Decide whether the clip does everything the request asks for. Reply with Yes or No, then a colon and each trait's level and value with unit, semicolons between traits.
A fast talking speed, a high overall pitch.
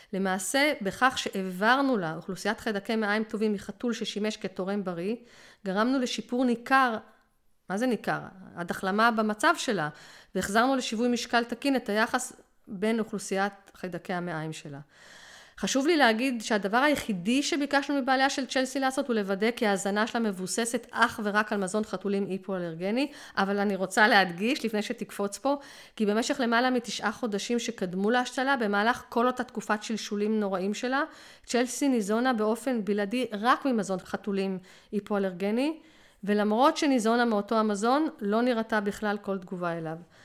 No: average, 140 wpm; high, 220 Hz